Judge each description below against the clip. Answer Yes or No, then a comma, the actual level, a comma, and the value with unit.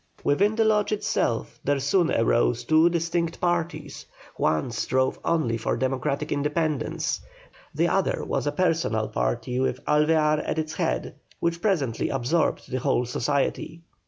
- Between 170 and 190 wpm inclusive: No, average, 140 wpm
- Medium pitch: Yes, medium, 150 Hz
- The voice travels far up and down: No, average, 4.6 semitones